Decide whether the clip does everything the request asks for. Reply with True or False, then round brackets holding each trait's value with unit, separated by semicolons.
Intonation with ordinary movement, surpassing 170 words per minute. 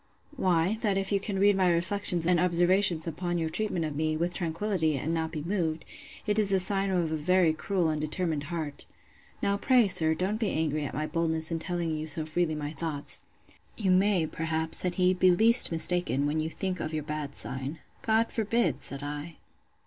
True (3.3 semitones; 200 wpm)